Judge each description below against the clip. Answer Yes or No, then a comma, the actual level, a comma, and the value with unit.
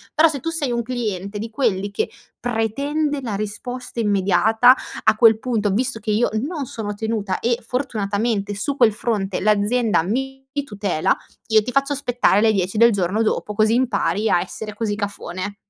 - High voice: Yes, high, 220 Hz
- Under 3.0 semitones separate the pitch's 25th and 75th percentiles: No, average, 3.3 semitones